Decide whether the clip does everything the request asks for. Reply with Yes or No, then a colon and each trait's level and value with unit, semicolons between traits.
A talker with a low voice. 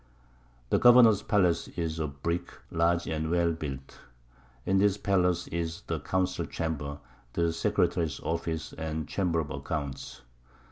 Yes: very low, 85 Hz